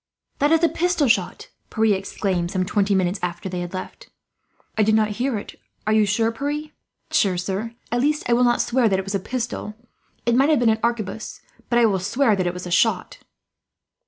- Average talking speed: No, fast, 215 wpm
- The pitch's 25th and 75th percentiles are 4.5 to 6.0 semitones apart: No, average, 4.1 semitones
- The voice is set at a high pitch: Yes, high, 220 Hz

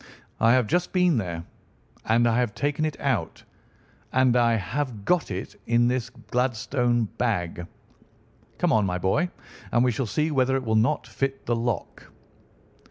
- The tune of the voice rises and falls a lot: No, average, 3.4 semitones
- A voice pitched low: Yes, low, 120 Hz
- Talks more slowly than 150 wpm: No, average, 165 wpm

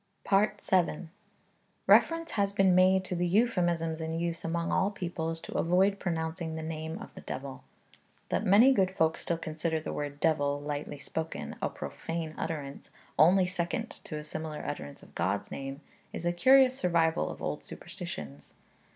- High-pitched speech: No, medium, 165 Hz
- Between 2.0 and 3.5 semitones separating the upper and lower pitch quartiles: Yes, average, 3.1 semitones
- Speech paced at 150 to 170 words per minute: Yes, average, 160 wpm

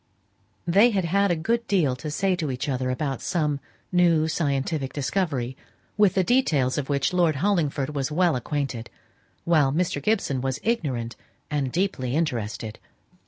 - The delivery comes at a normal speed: Yes, average, 155 wpm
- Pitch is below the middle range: No, medium, 150 Hz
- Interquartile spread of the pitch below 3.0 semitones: No, average, 5.2 semitones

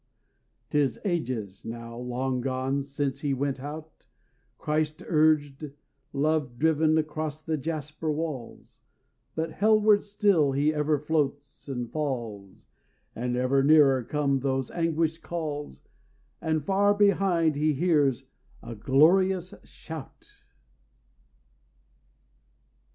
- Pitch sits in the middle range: Yes, medium, 150 Hz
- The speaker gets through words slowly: Yes, slow, 105 wpm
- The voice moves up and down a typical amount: Yes, average, 3.1 semitones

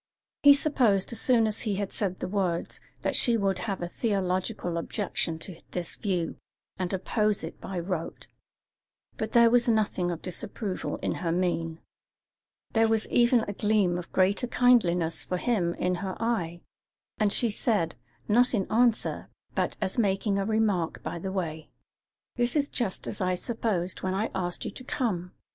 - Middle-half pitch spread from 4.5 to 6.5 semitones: No, average, 4.0 semitones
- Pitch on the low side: No, high, 195 Hz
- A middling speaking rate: Yes, average, 170 wpm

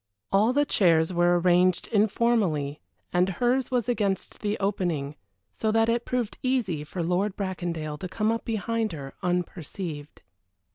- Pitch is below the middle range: No, high, 190 Hz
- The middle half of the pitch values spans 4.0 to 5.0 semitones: Yes, average, 4.7 semitones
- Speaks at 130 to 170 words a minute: Yes, average, 145 wpm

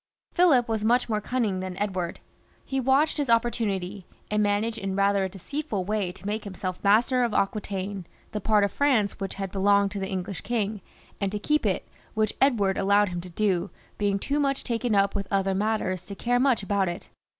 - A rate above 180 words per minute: Yes, average, 200 wpm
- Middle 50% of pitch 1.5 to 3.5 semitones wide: Yes, average, 3.0 semitones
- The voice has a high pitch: Yes, high, 205 Hz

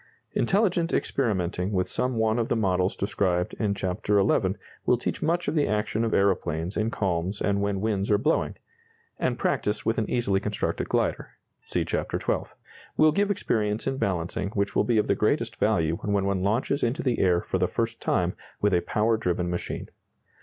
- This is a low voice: Yes, low, 105 Hz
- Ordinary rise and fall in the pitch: Yes, average, 3.6 semitones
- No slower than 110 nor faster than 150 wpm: No, average, 190 wpm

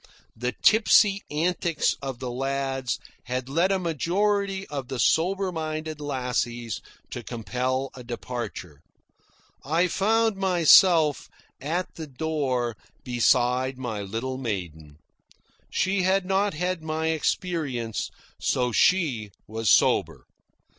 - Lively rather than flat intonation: Yes, wide, 6.4 semitones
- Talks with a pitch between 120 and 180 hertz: Yes, medium, 140 Hz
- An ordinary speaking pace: No, slow, 115 wpm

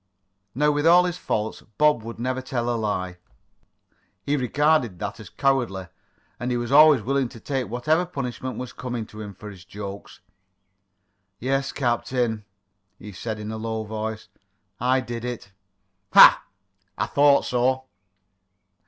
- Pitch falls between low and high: No, low, 120 Hz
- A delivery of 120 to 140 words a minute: No, average, 150 wpm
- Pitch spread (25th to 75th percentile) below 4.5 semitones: Yes, average, 3.8 semitones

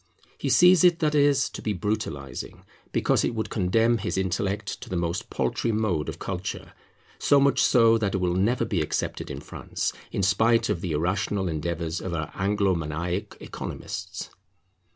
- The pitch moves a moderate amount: Yes, average, 4.6 semitones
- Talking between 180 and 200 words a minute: No, average, 170 wpm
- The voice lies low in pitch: Yes, low, 100 Hz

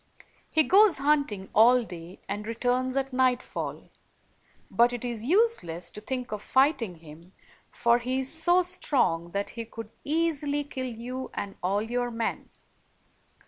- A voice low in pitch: No, high, 245 Hz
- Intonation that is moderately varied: Yes, average, 4.8 semitones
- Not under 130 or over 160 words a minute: Yes, average, 145 wpm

